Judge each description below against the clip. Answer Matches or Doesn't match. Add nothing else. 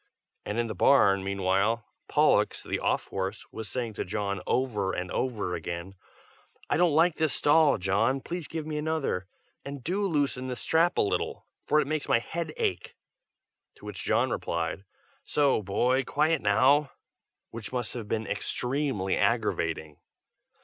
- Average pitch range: Doesn't match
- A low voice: Matches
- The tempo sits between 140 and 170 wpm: Matches